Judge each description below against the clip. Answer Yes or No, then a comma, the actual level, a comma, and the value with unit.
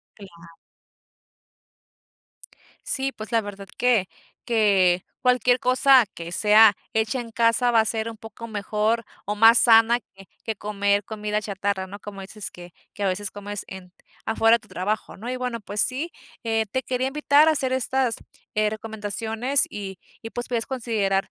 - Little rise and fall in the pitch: No, average, 3.1 semitones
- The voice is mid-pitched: No, high, 220 Hz